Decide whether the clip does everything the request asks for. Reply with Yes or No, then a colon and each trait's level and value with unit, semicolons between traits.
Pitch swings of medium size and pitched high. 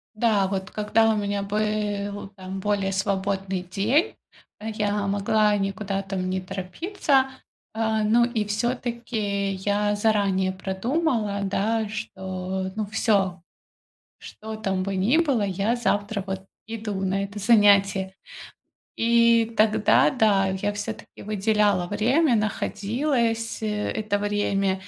No: narrow, 2.2 semitones; high, 205 Hz